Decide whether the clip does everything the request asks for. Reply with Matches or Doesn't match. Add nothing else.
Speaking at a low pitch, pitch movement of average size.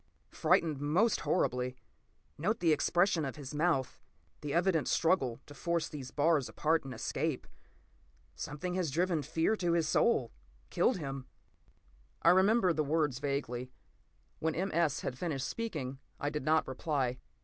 Doesn't match